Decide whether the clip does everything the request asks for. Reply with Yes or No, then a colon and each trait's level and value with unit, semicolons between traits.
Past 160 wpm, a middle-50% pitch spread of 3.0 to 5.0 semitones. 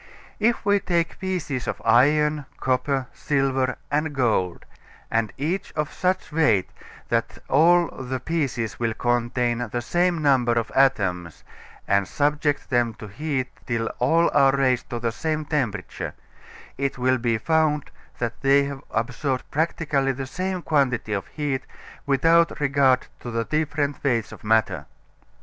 No: average, 145 wpm; average, 4.0 semitones